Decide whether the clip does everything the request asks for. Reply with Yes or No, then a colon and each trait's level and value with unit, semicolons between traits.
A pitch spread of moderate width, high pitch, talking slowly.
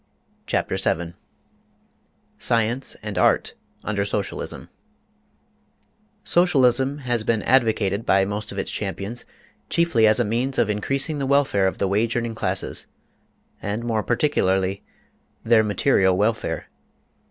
No: average, 3.7 semitones; low, 110 Hz; slow, 120 wpm